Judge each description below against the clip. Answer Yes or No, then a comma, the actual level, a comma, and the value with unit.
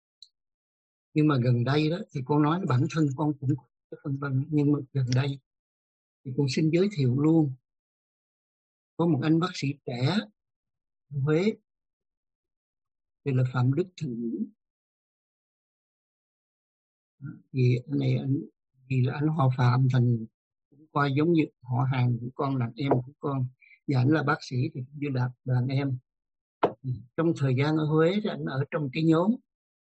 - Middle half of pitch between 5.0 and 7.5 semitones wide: No, average, 3.4 semitones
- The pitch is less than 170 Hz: Yes, medium, 140 Hz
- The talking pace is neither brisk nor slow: No, slow, 155 wpm